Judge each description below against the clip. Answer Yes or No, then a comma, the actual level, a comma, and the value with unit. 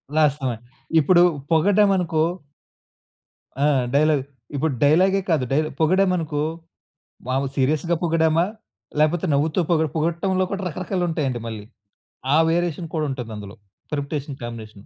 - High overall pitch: No, medium, 155 Hz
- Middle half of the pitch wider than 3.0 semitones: Yes, average, 3.7 semitones